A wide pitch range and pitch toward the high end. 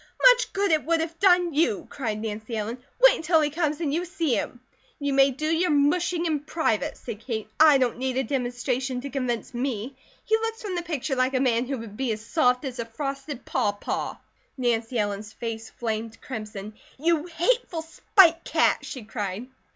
Yes: wide, 6.0 semitones; very high, 270 Hz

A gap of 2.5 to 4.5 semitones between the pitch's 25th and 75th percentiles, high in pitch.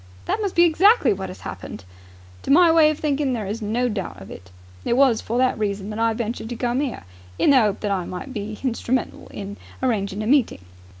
No: average, 5.0 semitones; high, 230 Hz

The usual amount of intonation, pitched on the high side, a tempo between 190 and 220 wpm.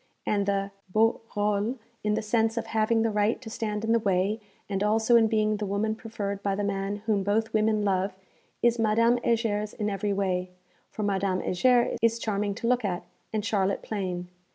No: narrow, 2.0 semitones; high, 210 Hz; average, 195 wpm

